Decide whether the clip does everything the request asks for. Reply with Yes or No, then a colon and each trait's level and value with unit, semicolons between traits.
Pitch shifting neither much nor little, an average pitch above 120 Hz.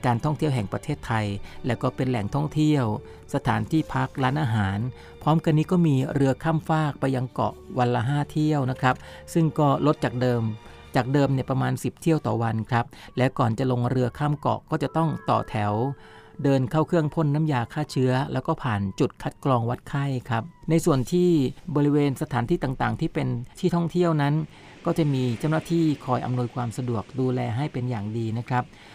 Yes: average, 3.8 semitones; low, 130 Hz